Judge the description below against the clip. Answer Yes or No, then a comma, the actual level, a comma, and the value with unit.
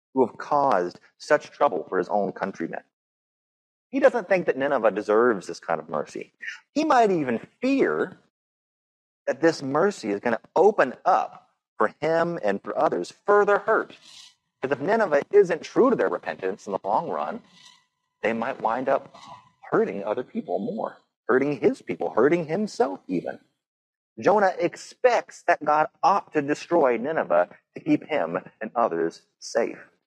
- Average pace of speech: Yes, average, 155 wpm